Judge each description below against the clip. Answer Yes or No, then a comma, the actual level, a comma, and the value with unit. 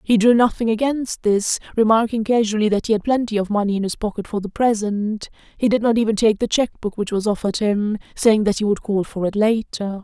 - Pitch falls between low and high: No, high, 215 Hz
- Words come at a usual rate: No, fast, 235 wpm